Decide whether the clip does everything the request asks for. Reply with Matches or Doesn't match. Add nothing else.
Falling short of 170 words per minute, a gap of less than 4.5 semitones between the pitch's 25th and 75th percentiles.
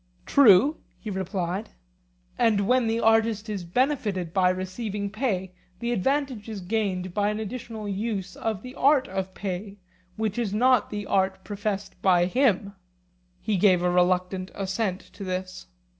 Matches